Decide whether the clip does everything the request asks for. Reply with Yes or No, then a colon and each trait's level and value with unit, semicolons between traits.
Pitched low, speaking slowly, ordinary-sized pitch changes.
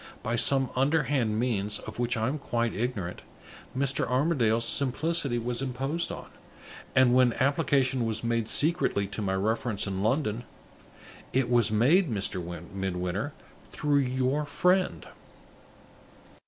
Yes: low, 125 Hz; slow, 125 wpm; average, 4.0 semitones